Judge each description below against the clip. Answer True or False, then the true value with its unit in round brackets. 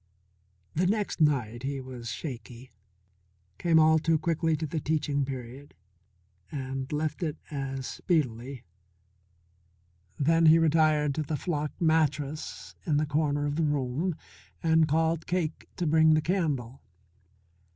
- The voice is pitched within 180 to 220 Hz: False (150 Hz)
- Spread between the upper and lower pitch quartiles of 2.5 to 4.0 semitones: True (2.9 semitones)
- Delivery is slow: True (130 wpm)